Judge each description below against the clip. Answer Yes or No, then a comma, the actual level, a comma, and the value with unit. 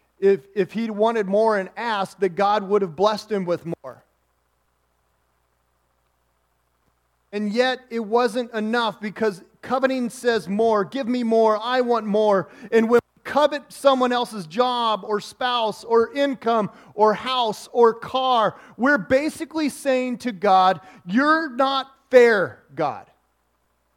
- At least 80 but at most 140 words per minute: Yes, slow, 135 wpm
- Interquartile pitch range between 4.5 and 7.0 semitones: Yes, average, 4.8 semitones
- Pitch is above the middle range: Yes, high, 220 Hz